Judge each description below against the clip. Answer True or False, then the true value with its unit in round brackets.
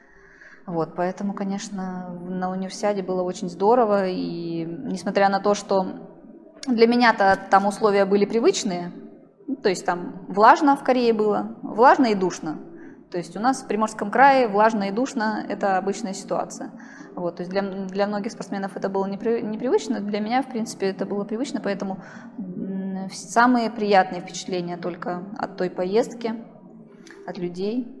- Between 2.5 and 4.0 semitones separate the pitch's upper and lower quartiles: True (3.5 semitones)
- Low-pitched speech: False (205 Hz)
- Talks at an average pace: True (150 wpm)